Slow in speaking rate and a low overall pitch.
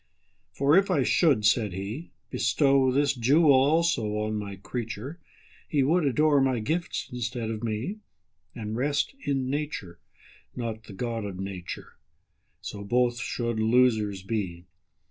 Yes: slow, 125 wpm; low, 120 Hz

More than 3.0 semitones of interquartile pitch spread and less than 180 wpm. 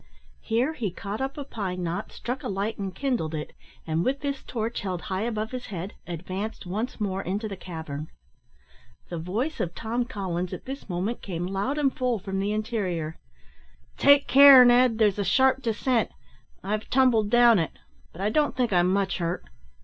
No: average, 5.2 semitones; average, 185 wpm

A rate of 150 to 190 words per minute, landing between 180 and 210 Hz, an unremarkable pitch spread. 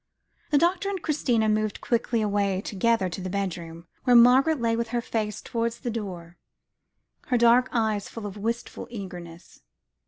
No: average, 160 wpm; high, 225 Hz; average, 3.4 semitones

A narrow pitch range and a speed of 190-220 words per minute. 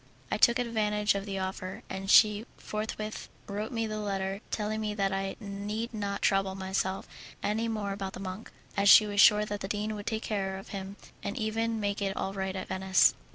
Yes: narrow, 1.7 semitones; fast, 205 wpm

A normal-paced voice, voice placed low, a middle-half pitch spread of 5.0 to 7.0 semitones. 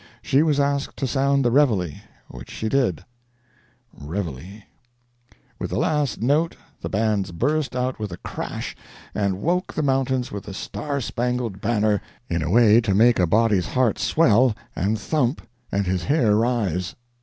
Yes: average, 170 wpm; low, 115 Hz; wide, 5.4 semitones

